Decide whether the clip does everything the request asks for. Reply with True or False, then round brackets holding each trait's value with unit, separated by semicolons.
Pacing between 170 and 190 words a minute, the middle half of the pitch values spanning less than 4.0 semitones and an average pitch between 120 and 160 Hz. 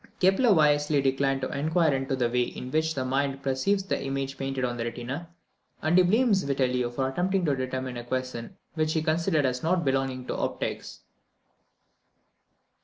True (175 wpm; 3.6 semitones; 135 Hz)